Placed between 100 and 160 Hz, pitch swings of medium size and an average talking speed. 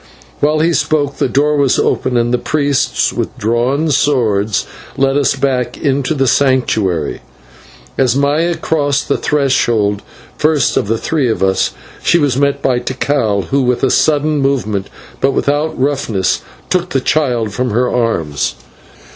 Yes: low, 135 Hz; average, 3.5 semitones; average, 155 wpm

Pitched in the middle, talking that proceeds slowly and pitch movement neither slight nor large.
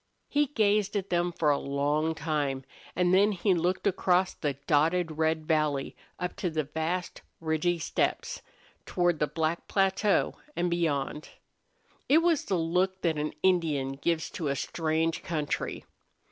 No: medium, 165 Hz; average, 150 wpm; average, 3.1 semitones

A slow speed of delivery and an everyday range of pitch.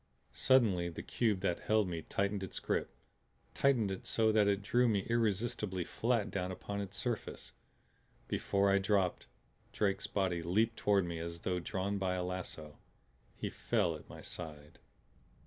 No: average, 160 wpm; average, 3.0 semitones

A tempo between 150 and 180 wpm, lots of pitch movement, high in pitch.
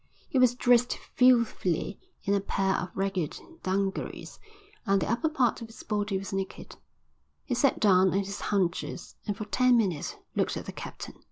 No: average, 175 wpm; average, 3.8 semitones; high, 200 Hz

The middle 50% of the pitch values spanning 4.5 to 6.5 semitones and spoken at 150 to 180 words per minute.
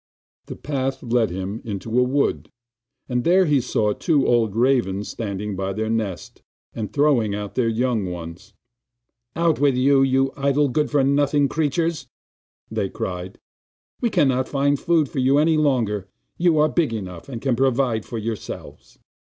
Yes: average, 4.9 semitones; average, 160 wpm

